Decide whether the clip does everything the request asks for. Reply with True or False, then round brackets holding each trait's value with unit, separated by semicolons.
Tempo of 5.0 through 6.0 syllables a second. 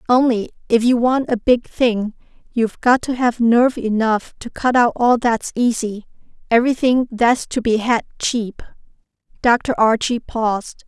False (4.4 syllables/s)